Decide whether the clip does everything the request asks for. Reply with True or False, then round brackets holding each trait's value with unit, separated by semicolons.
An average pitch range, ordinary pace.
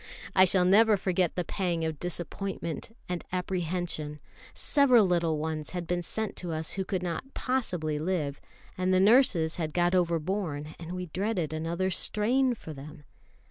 True (3.1 semitones; 160 wpm)